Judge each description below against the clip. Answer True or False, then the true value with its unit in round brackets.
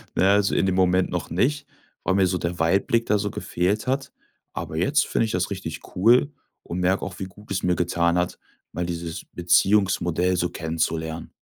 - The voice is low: True (90 Hz)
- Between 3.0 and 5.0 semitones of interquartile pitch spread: False (2.5 semitones)